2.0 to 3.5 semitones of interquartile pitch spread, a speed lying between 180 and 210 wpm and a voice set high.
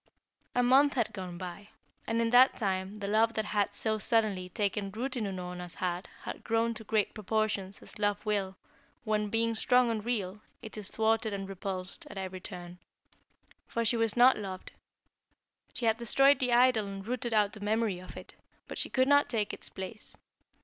Yes: average, 2.9 semitones; average, 190 wpm; high, 215 Hz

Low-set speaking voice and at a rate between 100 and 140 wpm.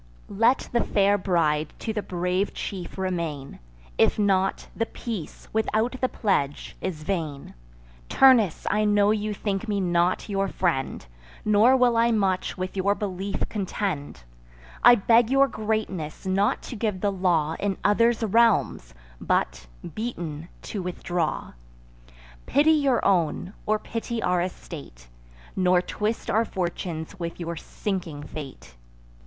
No: high, 195 Hz; slow, 135 wpm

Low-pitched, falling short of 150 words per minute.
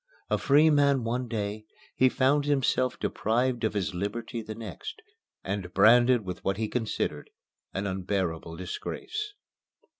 Yes: low, 115 Hz; average, 140 wpm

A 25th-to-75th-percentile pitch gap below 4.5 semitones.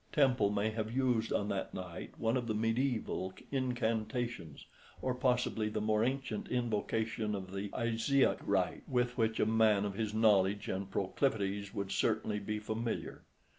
Yes: average, 2.9 semitones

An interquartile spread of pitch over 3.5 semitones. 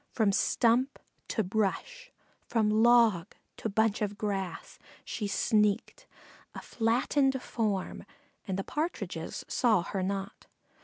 No: average, 3.2 semitones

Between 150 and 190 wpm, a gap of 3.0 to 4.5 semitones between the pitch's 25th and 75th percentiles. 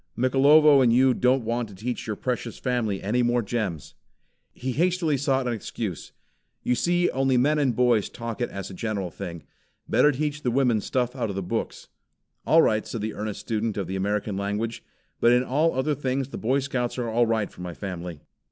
No: fast, 205 wpm; average, 4.0 semitones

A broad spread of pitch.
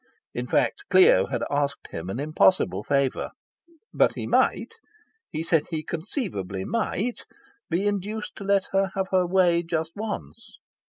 Yes: wide, 5.7 semitones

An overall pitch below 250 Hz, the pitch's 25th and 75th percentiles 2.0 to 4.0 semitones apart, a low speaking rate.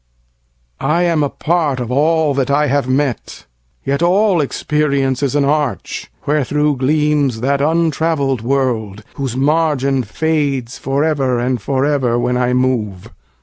Yes: medium, 140 Hz; average, 3.0 semitones; slow, 130 wpm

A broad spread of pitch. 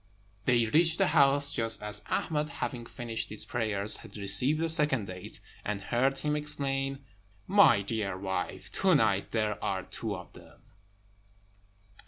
Yes: wide, 5.9 semitones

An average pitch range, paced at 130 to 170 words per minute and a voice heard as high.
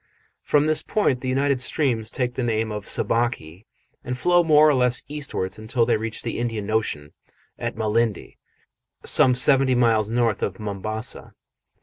No: average, 3.2 semitones; average, 155 wpm; low, 120 Hz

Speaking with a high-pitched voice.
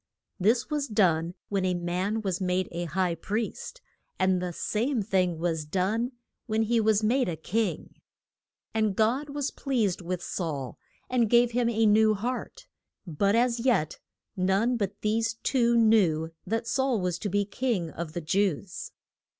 Yes: high, 205 Hz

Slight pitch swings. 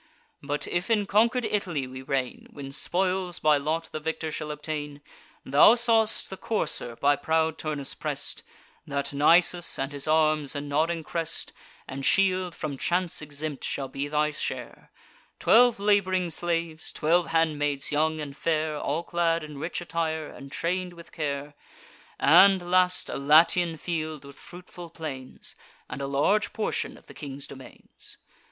No: average, 3.4 semitones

